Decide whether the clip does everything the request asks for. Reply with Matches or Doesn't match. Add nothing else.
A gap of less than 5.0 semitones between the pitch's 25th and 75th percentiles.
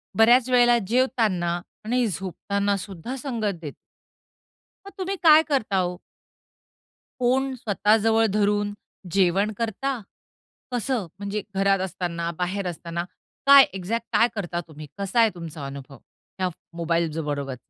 Doesn't match